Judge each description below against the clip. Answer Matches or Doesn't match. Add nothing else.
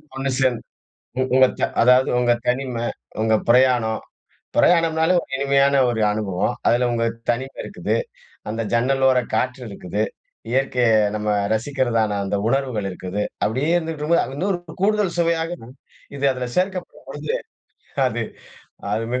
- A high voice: Doesn't match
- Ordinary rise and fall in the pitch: Matches